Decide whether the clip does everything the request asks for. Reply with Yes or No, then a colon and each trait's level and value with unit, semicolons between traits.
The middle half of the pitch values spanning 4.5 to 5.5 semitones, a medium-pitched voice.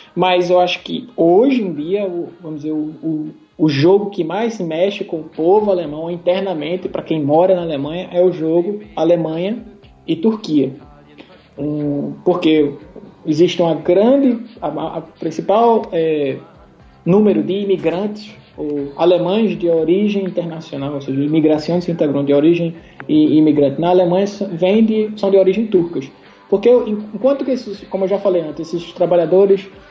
No: average, 3.8 semitones; medium, 175 Hz